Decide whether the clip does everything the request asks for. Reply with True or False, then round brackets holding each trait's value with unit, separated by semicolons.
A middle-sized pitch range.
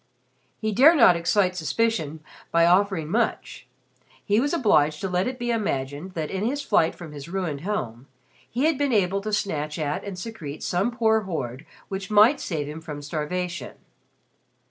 False (6.0 semitones)